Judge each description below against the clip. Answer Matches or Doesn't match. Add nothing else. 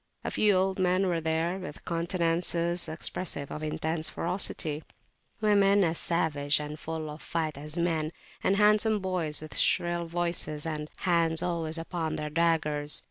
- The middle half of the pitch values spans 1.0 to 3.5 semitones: Matches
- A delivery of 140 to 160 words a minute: Matches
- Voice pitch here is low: Doesn't match